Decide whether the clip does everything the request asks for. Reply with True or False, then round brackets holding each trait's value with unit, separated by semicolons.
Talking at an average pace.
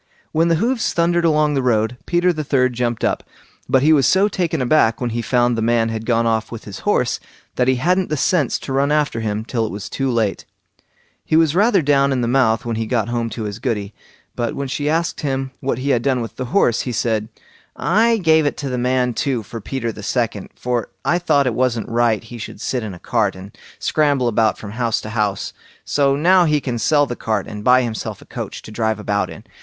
False (235 wpm)